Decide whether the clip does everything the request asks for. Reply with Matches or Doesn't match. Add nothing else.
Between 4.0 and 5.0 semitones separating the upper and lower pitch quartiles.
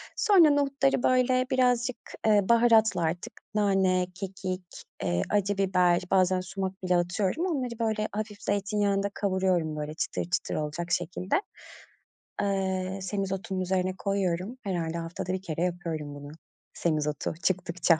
Doesn't match